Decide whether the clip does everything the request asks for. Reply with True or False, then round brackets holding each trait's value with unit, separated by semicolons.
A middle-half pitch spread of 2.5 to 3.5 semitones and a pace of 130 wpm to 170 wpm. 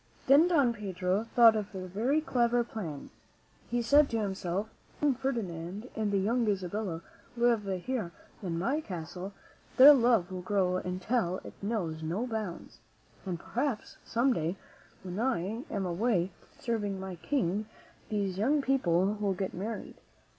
False (4.6 semitones; 155 wpm)